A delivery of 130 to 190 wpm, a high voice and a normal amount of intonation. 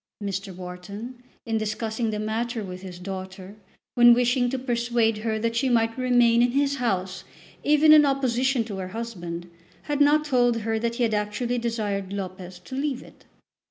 Yes: average, 175 wpm; high, 230 Hz; average, 3.6 semitones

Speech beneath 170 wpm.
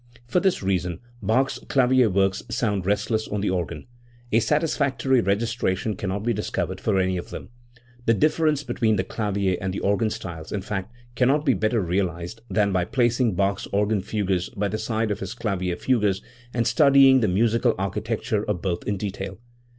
No: average, 180 wpm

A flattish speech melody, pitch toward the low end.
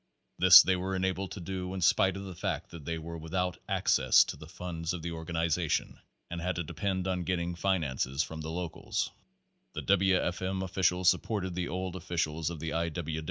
Yes: narrow, 2.2 semitones; very low, 90 Hz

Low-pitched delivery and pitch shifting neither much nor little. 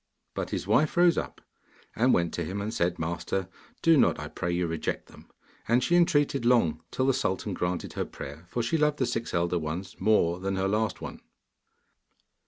No: very low, 95 Hz; wide, 6.4 semitones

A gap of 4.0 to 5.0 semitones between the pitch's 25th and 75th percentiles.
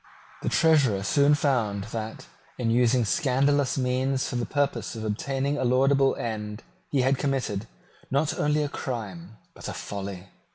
Yes: average, 4.3 semitones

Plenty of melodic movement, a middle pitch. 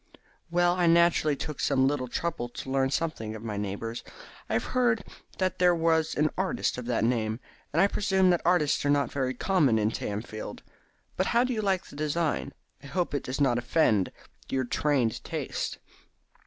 Yes: wide, 6.4 semitones; medium, 145 Hz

